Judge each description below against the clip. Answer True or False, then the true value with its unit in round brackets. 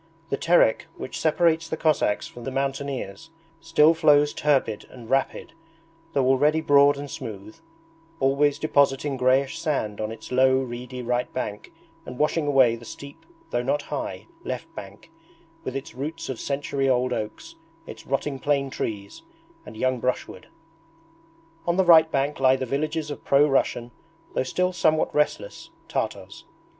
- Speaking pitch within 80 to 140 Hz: True (135 Hz)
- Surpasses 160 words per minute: False (150 wpm)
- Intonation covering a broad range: False (3.0 semitones)